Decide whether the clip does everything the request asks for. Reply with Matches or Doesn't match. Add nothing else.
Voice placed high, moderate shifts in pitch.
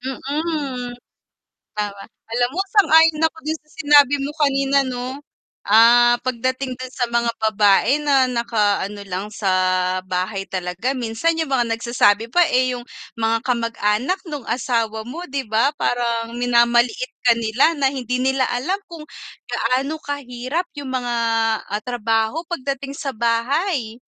Matches